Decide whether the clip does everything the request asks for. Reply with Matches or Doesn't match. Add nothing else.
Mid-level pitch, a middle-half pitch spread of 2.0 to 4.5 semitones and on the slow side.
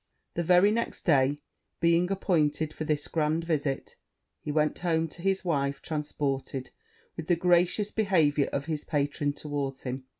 Doesn't match